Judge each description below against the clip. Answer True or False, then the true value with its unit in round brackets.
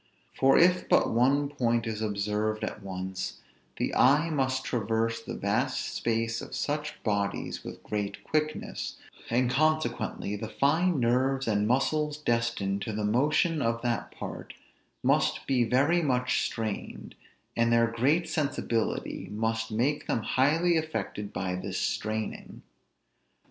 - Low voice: True (120 Hz)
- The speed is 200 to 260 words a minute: False (135 wpm)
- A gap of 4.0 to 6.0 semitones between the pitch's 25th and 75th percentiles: True (4.7 semitones)